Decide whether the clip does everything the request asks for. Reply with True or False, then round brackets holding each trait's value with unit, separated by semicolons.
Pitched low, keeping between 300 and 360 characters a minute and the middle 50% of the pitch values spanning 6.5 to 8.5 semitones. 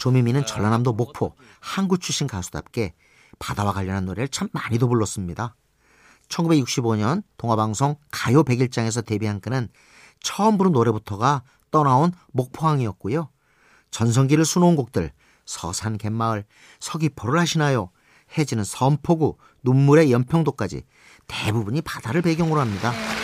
False (125 Hz; 310 characters per minute; 5.6 semitones)